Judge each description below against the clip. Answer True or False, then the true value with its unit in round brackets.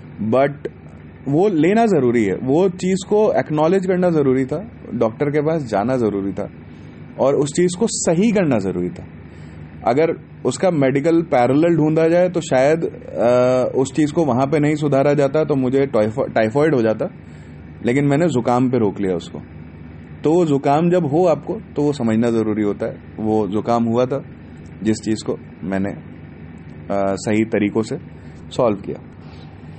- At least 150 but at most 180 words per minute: True (165 wpm)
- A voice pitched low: True (120 Hz)